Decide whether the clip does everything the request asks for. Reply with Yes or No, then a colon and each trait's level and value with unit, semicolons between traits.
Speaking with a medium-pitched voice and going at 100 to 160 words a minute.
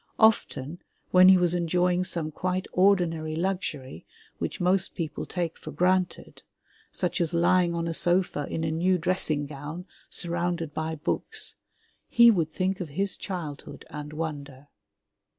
Yes: medium, 170 Hz; average, 145 wpm